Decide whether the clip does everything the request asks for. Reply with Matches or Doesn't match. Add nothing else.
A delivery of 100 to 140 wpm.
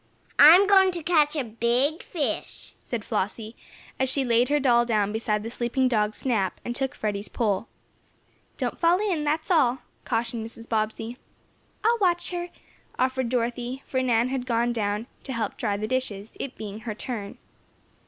Doesn't match